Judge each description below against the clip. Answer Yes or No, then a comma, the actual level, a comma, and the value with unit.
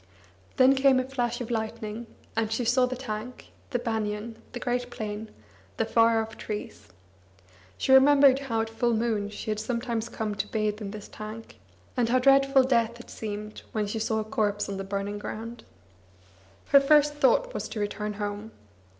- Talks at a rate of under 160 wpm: No, average, 180 wpm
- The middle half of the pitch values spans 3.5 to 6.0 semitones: No, average, 2.9 semitones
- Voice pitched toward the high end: Yes, high, 225 Hz